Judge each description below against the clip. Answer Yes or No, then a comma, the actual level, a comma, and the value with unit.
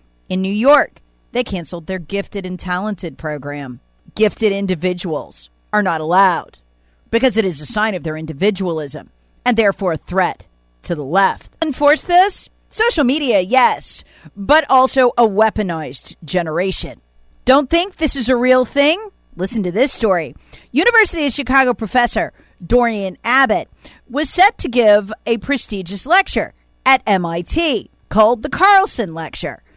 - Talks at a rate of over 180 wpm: No, average, 140 wpm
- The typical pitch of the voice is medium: No, high, 210 Hz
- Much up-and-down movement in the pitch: Yes, wide, 7.5 semitones